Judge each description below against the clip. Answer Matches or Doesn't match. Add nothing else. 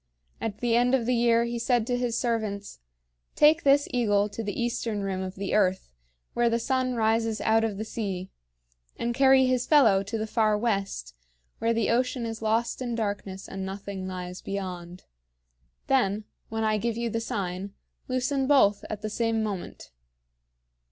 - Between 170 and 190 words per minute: Matches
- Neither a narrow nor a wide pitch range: Matches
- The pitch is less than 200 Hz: Doesn't match